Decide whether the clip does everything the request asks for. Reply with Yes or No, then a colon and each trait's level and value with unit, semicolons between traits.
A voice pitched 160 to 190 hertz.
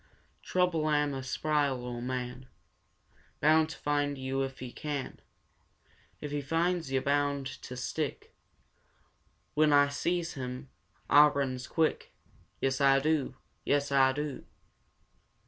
No: medium, 140 Hz